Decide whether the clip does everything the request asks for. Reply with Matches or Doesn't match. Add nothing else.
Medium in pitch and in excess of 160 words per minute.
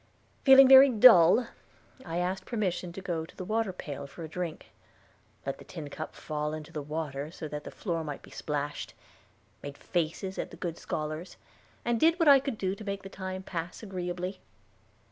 Matches